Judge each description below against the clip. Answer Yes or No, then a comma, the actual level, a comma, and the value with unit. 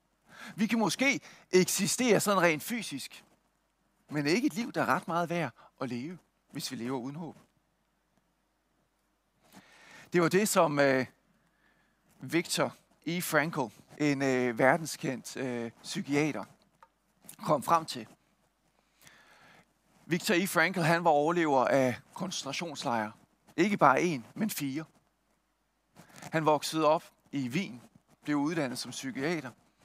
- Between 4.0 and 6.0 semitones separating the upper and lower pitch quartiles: Yes, average, 4.9 semitones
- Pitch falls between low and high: Yes, medium, 160 Hz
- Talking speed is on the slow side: Yes, slow, 125 wpm